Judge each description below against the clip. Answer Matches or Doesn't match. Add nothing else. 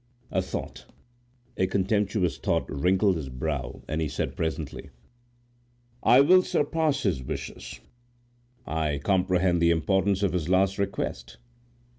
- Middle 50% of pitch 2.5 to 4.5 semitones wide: Matches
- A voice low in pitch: Matches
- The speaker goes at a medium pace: Doesn't match